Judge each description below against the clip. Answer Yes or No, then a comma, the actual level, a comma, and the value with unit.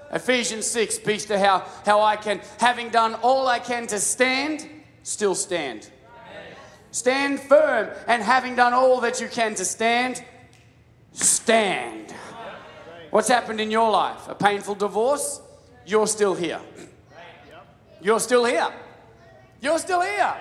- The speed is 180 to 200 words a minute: No, slow, 135 wpm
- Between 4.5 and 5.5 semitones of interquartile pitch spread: No, average, 3.8 semitones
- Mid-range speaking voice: No, high, 225 Hz